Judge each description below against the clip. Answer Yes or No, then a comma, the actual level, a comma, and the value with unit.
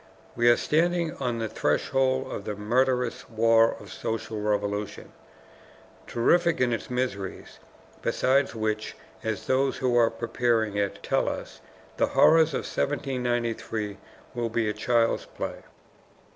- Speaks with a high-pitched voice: No, low, 120 Hz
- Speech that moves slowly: Yes, slow, 130 wpm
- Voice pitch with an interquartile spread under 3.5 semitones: Yes, average, 3.1 semitones